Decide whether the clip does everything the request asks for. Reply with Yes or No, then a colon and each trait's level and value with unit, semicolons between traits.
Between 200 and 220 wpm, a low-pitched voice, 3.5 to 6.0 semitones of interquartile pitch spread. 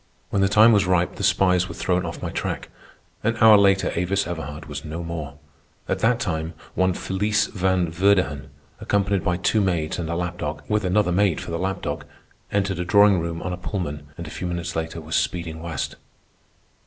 No: fast, 205 wpm; very low, 90 Hz; average, 3.0 semitones